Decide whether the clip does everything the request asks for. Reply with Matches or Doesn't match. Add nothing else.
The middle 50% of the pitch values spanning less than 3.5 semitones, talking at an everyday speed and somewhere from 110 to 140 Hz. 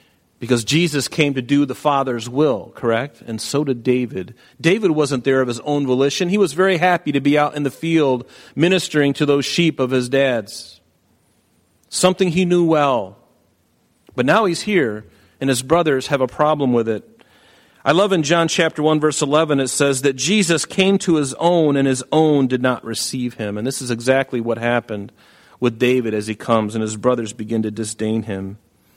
Doesn't match